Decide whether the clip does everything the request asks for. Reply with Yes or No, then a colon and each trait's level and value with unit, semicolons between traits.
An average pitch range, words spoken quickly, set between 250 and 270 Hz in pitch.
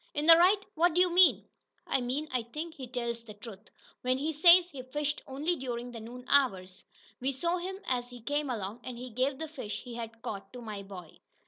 Yes: average, 4.7 semitones; fast, 225 wpm; very high, 255 Hz